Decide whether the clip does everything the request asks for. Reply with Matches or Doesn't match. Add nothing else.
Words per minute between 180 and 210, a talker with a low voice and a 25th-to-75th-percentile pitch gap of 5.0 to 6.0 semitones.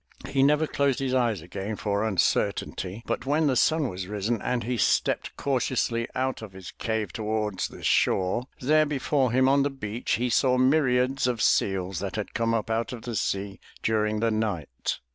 Doesn't match